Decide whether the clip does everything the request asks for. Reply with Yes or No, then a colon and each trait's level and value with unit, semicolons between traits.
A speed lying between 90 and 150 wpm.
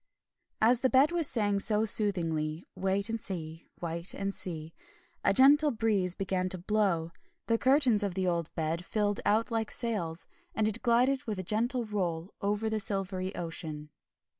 No: average, 165 wpm